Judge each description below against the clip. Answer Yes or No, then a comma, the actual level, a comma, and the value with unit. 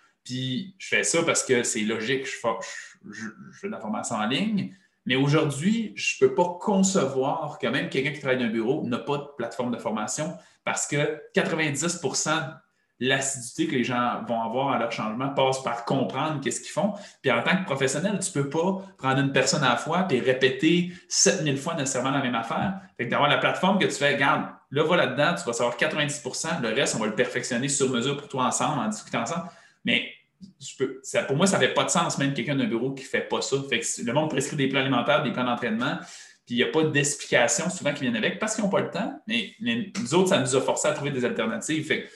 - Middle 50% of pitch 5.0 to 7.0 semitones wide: Yes, wide, 5.6 semitones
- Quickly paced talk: Yes, fast, 240 wpm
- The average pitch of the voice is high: No, medium, 145 Hz